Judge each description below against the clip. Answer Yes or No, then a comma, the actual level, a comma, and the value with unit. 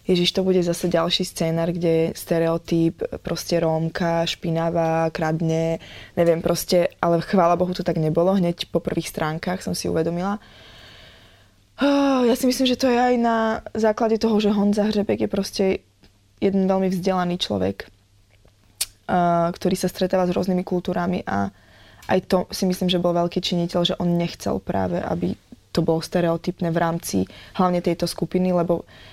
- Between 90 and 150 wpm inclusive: No, average, 160 wpm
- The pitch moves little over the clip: Yes, narrow, 2.3 semitones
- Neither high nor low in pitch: Yes, medium, 175 Hz